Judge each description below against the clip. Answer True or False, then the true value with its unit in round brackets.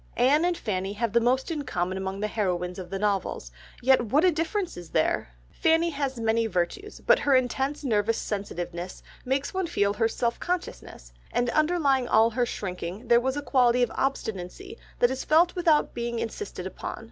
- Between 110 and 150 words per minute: False (185 wpm)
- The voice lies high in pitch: True (240 Hz)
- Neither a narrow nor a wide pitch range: False (6.4 semitones)